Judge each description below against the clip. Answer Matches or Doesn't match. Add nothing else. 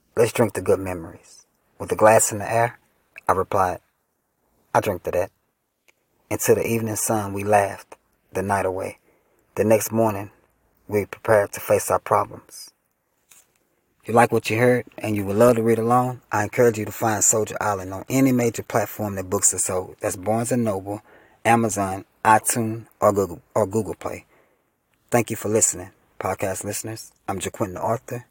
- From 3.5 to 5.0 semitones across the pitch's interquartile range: Doesn't match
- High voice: Doesn't match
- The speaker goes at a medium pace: Matches